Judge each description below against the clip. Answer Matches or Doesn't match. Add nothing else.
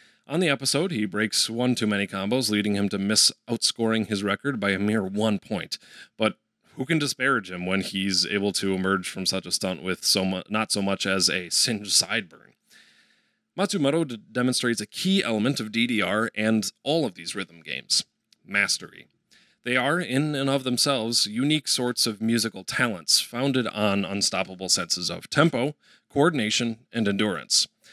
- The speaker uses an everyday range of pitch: Matches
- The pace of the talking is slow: Doesn't match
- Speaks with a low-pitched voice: Matches